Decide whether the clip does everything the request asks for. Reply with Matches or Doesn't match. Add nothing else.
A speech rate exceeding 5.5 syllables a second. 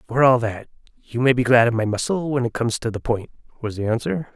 Matches